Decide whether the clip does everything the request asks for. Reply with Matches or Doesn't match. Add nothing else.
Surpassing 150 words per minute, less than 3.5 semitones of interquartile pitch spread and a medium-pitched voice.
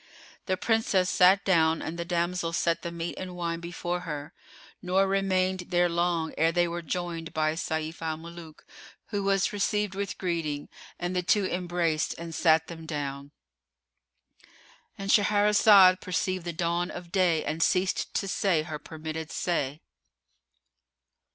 Doesn't match